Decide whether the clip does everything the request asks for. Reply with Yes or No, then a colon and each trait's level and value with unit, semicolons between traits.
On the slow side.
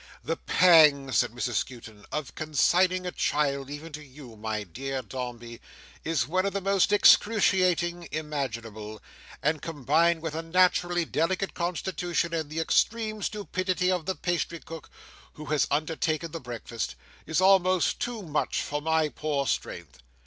No: average, 150 wpm